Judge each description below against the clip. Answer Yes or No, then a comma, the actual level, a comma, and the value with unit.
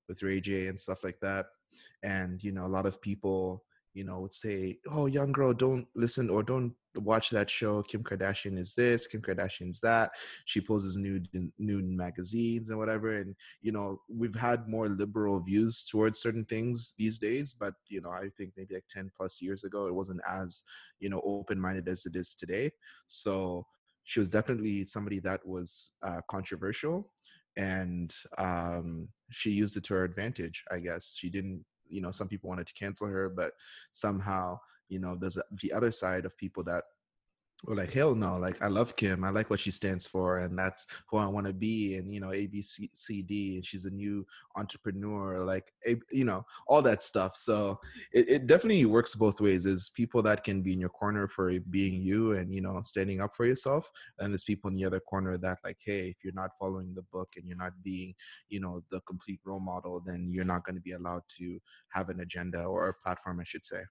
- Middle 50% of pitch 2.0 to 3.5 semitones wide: Yes, narrow, 2.4 semitones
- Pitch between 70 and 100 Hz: Yes, very low, 95 Hz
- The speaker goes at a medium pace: No, fast, 210 wpm